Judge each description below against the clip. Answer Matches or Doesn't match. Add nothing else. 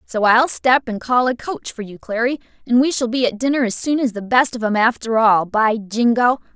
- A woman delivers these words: Matches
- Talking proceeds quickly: Matches